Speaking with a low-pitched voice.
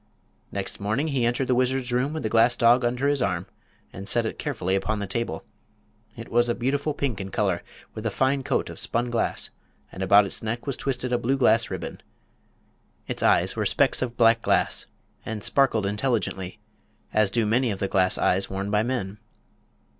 Yes: low, 115 Hz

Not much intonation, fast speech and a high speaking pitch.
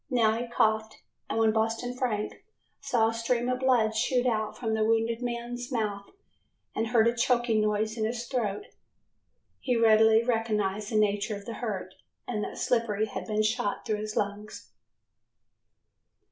No: narrow, 1.9 semitones; average, 160 wpm; high, 225 Hz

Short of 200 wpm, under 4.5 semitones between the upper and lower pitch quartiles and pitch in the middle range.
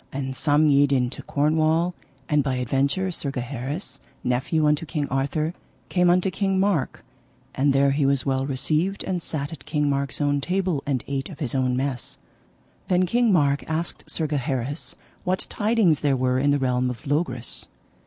Yes: average, 175 wpm; average, 3.6 semitones; medium, 145 Hz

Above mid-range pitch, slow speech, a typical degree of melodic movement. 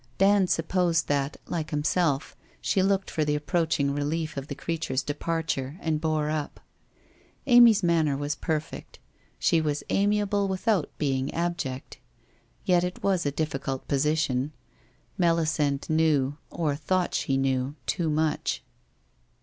No: medium, 155 Hz; slow, 130 wpm; average, 3.3 semitones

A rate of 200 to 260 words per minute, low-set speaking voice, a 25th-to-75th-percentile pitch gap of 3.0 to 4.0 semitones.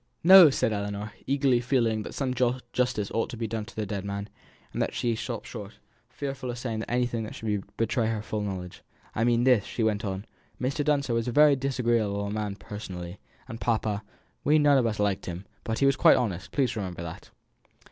Yes: fast, 205 wpm; low, 115 Hz; average, 3.5 semitones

